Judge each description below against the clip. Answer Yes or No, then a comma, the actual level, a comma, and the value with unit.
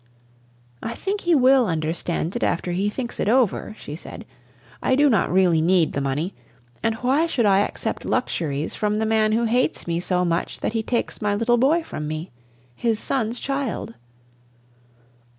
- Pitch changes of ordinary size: No, wide, 6.1 semitones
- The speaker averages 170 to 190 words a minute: Yes, average, 175 wpm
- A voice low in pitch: No, high, 215 Hz